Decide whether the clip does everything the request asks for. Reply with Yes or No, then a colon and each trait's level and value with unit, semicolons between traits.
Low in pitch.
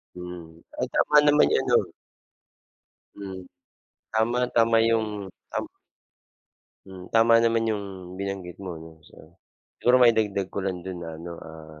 Yes: low, 100 Hz